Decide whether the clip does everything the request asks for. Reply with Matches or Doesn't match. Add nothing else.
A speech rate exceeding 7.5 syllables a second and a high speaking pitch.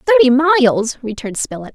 Matches